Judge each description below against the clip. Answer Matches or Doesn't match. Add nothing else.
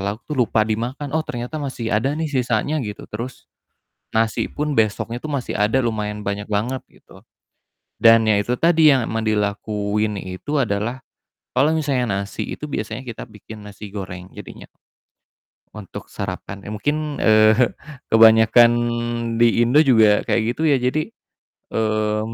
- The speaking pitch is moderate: Doesn't match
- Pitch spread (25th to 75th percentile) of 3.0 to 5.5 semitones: Matches